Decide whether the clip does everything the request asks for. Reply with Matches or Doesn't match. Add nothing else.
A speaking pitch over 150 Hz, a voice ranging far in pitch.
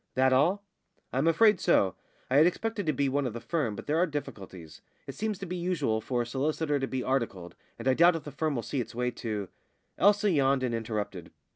Doesn't match